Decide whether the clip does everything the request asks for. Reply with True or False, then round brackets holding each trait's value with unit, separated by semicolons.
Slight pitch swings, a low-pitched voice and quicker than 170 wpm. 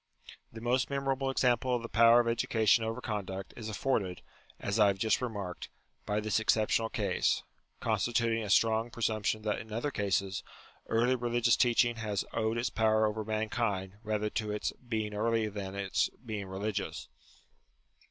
False (2.1 semitones; 110 Hz; 165 wpm)